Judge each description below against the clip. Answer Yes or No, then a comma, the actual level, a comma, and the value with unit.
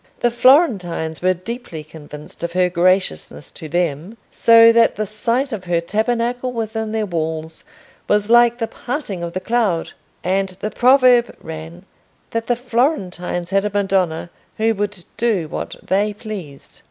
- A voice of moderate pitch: No, high, 200 Hz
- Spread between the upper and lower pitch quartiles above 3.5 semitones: Yes, average, 5.2 semitones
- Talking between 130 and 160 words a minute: Yes, average, 155 wpm